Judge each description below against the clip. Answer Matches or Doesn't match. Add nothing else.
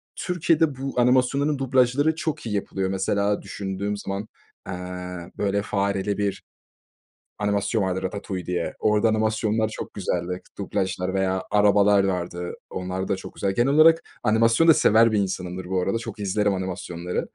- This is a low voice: Matches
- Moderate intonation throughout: Matches